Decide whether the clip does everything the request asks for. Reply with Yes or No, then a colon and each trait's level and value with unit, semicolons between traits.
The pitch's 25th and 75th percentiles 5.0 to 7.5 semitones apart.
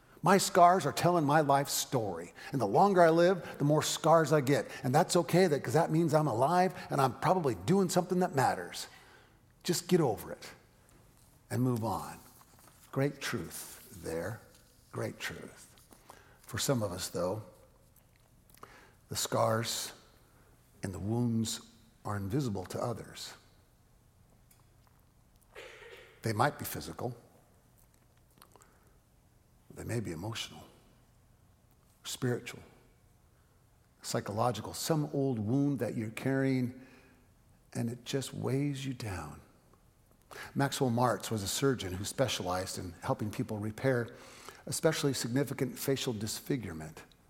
Yes: average, 5.3 semitones